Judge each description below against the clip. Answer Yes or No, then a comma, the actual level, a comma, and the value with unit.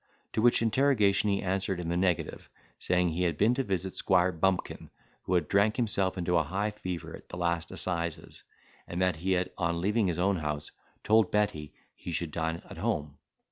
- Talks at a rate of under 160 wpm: No, average, 195 wpm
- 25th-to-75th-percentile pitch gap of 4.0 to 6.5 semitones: No, average, 2.8 semitones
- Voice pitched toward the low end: Yes, very low, 90 Hz